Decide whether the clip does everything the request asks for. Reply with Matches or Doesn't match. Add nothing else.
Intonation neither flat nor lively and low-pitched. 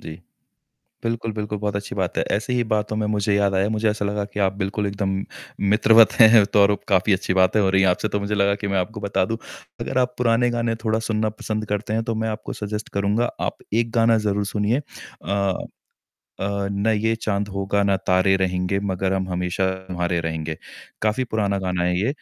Doesn't match